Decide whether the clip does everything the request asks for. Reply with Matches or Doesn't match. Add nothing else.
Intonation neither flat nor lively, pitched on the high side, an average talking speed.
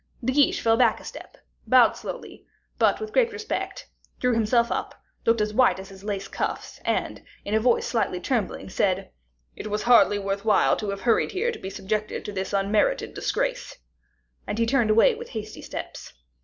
Matches